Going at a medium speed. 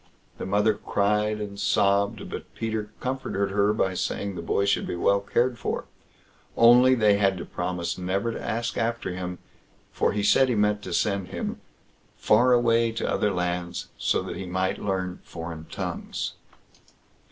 Yes: average, 165 wpm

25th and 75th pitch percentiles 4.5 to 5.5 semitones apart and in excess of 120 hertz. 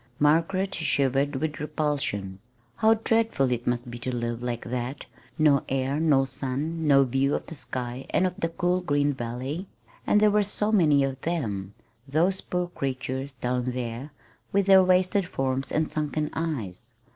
Yes: average, 4.8 semitones; medium, 140 Hz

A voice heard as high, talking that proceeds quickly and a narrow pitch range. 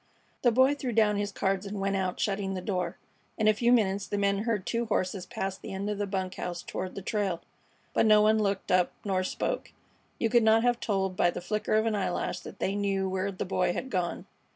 Yes: high, 200 Hz; fast, 235 wpm; narrow, 2.3 semitones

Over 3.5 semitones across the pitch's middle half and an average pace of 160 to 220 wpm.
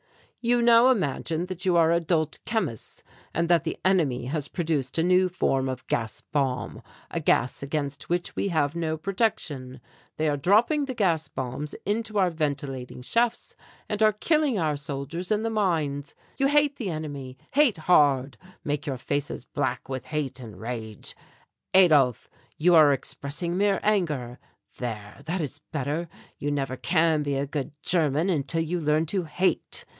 Yes: average, 4.9 semitones; average, 165 wpm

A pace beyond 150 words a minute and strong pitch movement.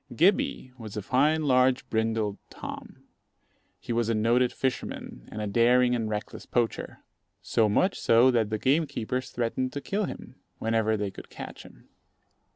No: average, 160 wpm; average, 2.8 semitones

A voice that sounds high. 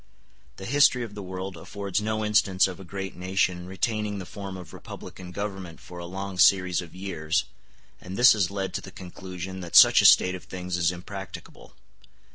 No: very low, 95 Hz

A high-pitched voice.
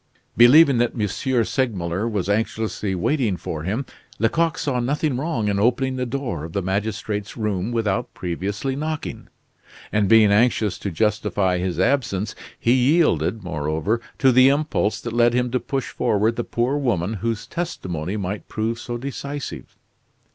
No: low, 115 Hz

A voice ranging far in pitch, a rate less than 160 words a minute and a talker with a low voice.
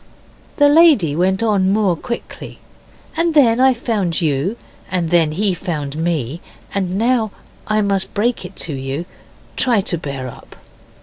No: wide, 5.8 semitones; average, 150 wpm; high, 190 Hz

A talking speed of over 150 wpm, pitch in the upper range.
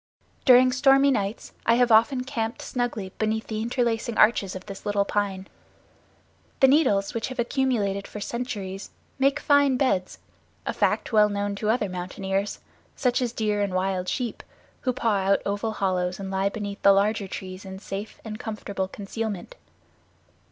Yes: average, 160 wpm; high, 210 Hz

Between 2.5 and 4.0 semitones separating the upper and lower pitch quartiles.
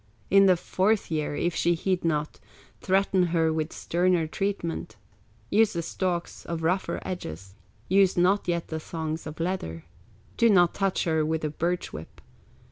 Yes: average, 2.8 semitones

